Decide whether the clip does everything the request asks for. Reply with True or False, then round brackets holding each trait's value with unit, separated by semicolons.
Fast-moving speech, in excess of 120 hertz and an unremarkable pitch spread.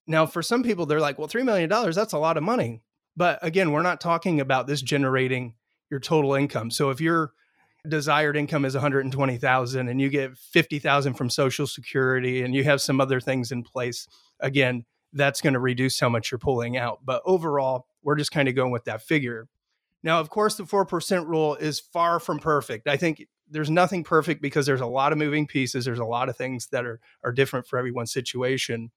True (210 wpm; 140 Hz; 3.6 semitones)